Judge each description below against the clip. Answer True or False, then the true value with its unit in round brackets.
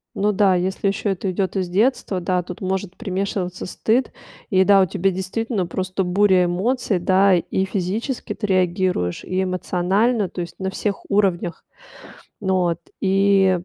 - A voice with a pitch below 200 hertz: True (190 Hz)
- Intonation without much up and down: True (1.7 semitones)